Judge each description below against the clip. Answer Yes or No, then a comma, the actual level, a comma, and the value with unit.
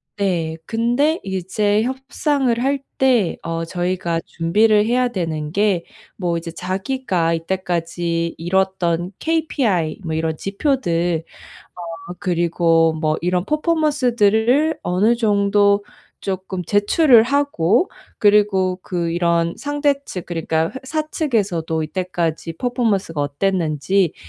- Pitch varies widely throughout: Yes, wide, 5.9 semitones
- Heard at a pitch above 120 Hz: Yes, high, 190 Hz